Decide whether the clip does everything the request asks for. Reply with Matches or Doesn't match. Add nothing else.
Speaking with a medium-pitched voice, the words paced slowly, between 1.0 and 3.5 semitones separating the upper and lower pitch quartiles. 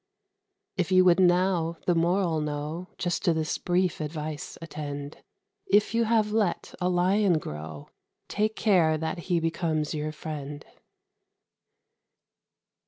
Matches